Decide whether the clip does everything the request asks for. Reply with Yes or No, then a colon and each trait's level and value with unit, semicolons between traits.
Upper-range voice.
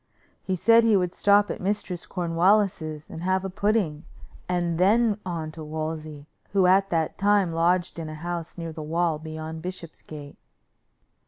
No: medium, 175 Hz